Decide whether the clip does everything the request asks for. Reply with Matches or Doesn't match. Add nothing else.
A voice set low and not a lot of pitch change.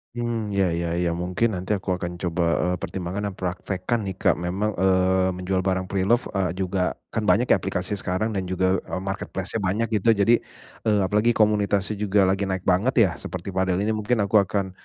Matches